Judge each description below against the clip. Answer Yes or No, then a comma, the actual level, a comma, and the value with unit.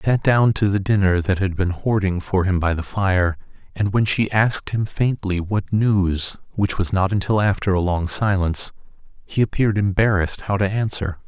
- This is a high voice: No, low, 100 Hz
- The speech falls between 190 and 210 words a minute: Yes, average, 195 wpm